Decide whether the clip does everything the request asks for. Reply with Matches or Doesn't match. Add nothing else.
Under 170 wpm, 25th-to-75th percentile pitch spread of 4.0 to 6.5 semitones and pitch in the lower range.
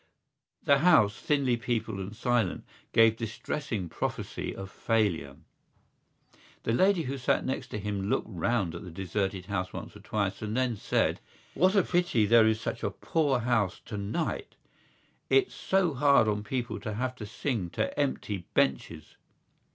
Matches